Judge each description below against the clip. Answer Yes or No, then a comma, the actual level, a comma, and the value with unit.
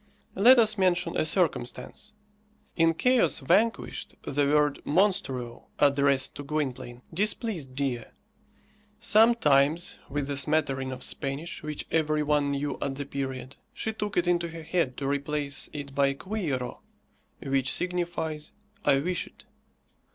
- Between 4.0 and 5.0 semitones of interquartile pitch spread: Yes, average, 4.3 semitones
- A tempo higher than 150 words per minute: No, slow, 135 wpm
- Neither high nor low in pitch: Yes, medium, 150 Hz